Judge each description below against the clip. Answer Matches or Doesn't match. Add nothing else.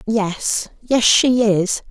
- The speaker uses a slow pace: Matches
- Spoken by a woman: Matches